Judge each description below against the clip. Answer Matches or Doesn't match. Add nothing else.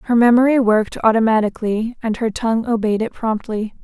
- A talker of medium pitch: Doesn't match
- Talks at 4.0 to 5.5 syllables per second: Doesn't match